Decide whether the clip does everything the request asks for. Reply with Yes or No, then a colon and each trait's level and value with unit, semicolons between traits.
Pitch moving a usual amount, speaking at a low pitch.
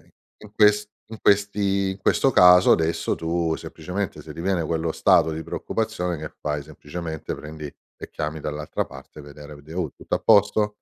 Yes: average, 4.4 semitones; very low, 85 Hz